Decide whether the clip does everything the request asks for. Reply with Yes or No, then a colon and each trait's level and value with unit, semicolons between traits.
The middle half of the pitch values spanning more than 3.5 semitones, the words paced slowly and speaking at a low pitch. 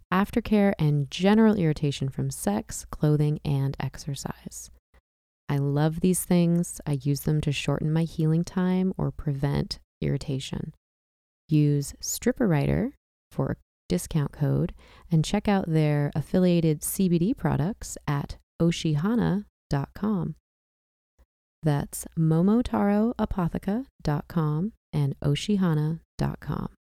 No: average, 4.6 semitones; slow, 95 wpm; medium, 155 Hz